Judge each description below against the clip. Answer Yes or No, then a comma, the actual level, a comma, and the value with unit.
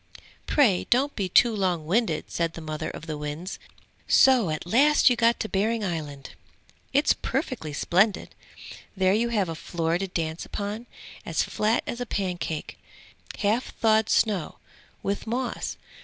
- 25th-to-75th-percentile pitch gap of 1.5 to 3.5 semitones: No, wide, 5.6 semitones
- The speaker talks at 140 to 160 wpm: Yes, average, 155 wpm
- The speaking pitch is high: Yes, high, 195 Hz